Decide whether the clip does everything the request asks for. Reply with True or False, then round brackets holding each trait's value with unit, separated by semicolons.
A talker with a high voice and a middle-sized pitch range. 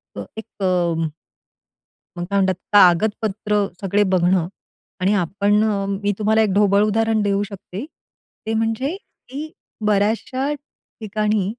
False (210 Hz; 2.0 semitones)